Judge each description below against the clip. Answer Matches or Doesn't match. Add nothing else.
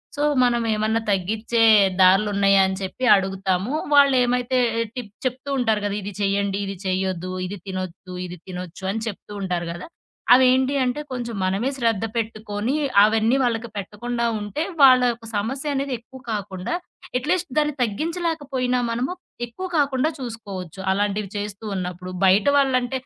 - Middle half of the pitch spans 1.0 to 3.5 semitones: Doesn't match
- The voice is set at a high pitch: Matches